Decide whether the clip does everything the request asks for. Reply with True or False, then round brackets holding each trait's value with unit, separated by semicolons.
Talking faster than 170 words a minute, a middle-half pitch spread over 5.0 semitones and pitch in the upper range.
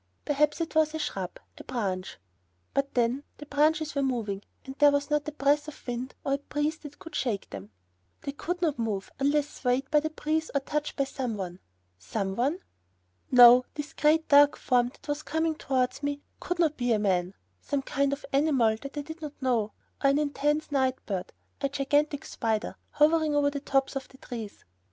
False (200 wpm; 3.4 semitones; 280 Hz)